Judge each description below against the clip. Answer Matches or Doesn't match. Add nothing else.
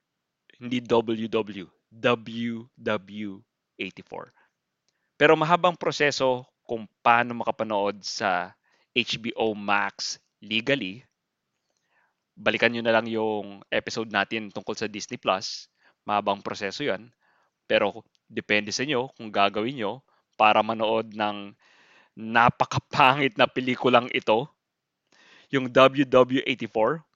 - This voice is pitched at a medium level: Doesn't match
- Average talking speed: Doesn't match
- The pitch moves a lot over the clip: Doesn't match